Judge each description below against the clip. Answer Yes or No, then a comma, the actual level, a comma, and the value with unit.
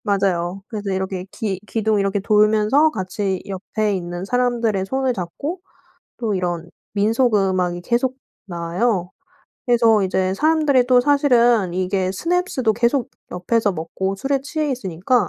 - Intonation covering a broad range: No, average, 4.7 semitones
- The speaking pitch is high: Yes, high, 210 Hz